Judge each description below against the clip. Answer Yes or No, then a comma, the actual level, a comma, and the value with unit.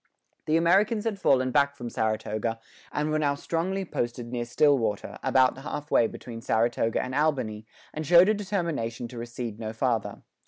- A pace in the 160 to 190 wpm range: Yes, average, 165 wpm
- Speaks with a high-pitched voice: No, low, 130 Hz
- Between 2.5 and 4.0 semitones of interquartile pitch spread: No, wide, 5.4 semitones